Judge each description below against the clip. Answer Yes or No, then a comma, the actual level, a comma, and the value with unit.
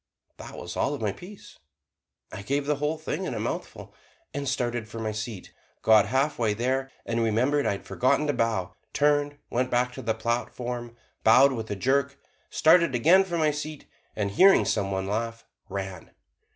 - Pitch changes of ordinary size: Yes, average, 4.7 semitones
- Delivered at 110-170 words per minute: No, average, 180 wpm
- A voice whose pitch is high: No, low, 125 Hz